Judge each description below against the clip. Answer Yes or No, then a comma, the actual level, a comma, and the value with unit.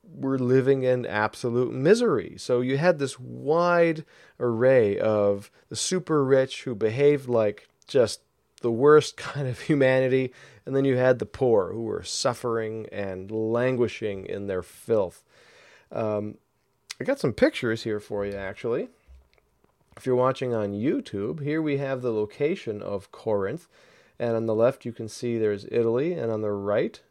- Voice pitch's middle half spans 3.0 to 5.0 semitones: Yes, average, 3.6 semitones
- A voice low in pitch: Yes, low, 120 Hz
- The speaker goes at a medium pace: Yes, average, 160 wpm